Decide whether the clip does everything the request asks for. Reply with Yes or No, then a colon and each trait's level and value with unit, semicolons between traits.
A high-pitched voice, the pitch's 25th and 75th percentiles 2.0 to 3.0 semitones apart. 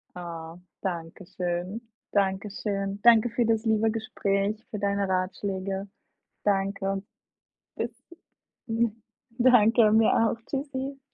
Yes: high, 205 Hz; average, 2.7 semitones